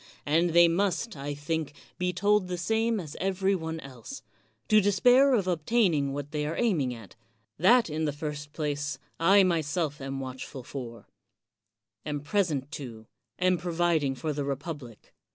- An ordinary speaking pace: Yes, average, 160 wpm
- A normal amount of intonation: Yes, average, 4.5 semitones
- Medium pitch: Yes, medium, 160 Hz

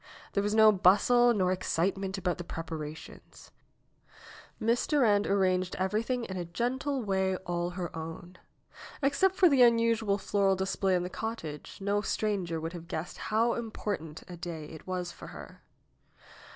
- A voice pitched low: No, high, 195 Hz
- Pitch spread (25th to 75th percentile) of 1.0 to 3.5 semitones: No, average, 4.1 semitones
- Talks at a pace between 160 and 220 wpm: No, average, 150 wpm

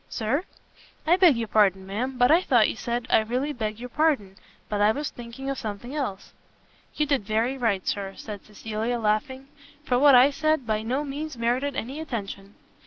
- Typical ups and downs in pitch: Yes, average, 4.4 semitones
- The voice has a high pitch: Yes, high, 240 Hz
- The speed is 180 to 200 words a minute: Yes, average, 190 wpm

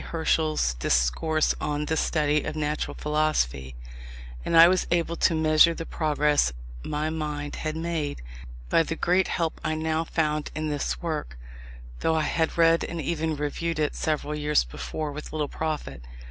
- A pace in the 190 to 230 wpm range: No, average, 160 wpm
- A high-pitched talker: No, medium, 155 Hz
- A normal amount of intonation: No, narrow, 1.5 semitones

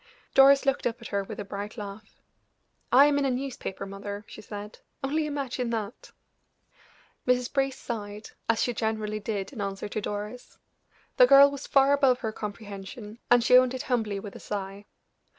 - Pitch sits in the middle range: No, high, 225 Hz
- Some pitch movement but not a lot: Yes, average, 4.3 semitones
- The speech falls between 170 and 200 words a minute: Yes, average, 180 wpm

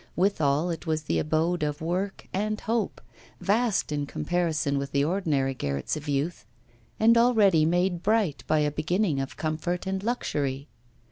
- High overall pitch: No, medium, 165 Hz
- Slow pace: No, average, 155 wpm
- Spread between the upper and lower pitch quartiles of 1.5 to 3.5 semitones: No, average, 4.7 semitones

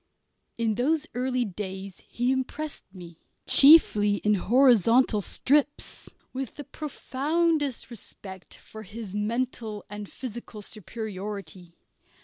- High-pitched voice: Yes, high, 230 Hz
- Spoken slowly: Yes, slow, 105 wpm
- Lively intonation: No, average, 4.4 semitones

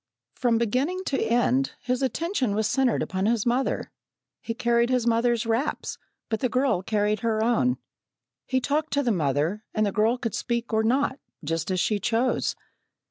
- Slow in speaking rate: No, average, 175 wpm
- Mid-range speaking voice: No, high, 235 Hz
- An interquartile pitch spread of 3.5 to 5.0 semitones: No, average, 2.9 semitones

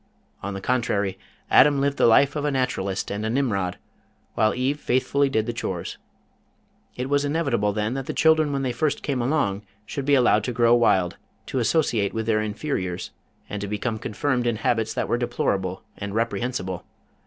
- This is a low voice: Yes, low, 120 Hz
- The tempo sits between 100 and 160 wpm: No, average, 185 wpm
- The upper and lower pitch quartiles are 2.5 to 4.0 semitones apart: No, average, 4.8 semitones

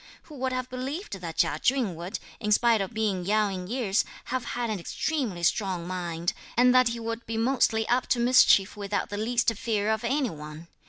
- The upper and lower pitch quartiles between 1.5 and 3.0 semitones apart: No, average, 4.5 semitones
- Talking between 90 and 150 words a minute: No, fast, 205 wpm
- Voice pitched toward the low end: No, high, 220 Hz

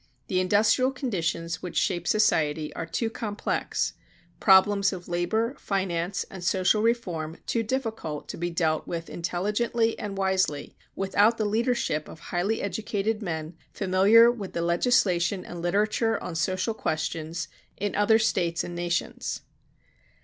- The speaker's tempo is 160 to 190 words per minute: No, slow, 135 wpm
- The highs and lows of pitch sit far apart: No, average, 4.2 semitones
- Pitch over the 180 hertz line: Yes, high, 190 Hz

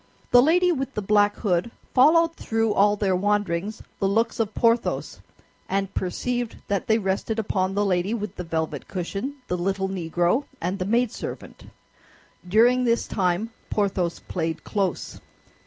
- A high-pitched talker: Yes, high, 205 Hz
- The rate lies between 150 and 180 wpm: Yes, average, 155 wpm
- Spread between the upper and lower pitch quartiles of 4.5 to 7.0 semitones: No, average, 3.9 semitones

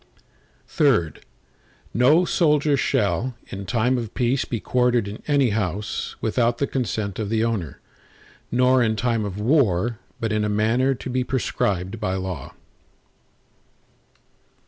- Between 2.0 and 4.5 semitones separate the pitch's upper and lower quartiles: Yes, average, 3.7 semitones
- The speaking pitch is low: Yes, low, 115 Hz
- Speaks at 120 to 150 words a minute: Yes, slow, 135 wpm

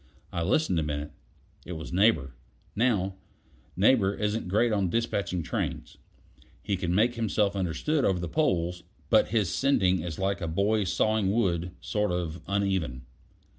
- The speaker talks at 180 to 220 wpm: No, average, 150 wpm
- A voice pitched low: Yes, very low, 95 Hz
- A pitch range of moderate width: Yes, average, 3.7 semitones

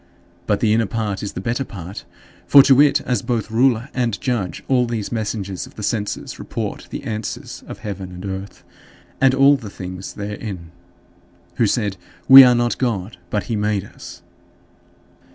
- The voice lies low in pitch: Yes, low, 110 Hz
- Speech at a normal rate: Yes, average, 170 wpm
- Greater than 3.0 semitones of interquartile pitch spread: Yes, average, 3.6 semitones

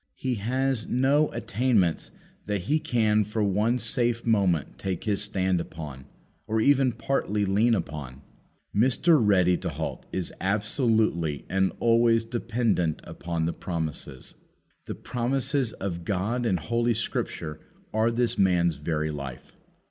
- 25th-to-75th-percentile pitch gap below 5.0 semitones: No, average, 5.3 semitones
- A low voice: Yes, low, 105 Hz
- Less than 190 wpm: Yes, slow, 135 wpm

